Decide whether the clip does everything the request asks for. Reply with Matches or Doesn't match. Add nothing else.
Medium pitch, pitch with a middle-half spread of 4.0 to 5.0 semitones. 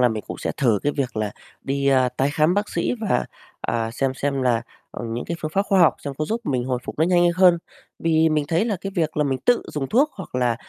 Doesn't match